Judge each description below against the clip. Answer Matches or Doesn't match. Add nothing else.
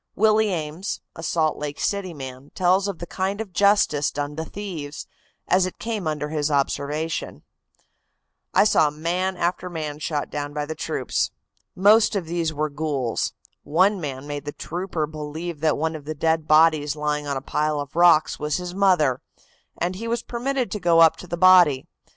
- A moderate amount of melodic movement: Matches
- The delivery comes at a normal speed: Matches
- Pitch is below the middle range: Doesn't match